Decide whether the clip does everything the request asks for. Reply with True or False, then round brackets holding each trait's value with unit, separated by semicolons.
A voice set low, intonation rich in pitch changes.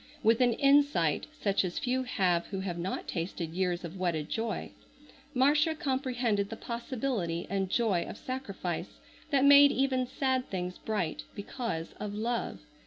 False (220 Hz; 6.2 semitones)